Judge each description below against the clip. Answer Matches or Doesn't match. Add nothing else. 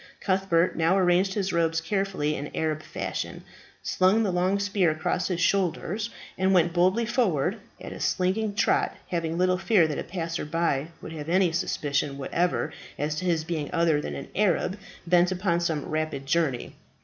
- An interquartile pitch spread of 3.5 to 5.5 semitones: Doesn't match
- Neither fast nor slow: Matches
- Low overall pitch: Doesn't match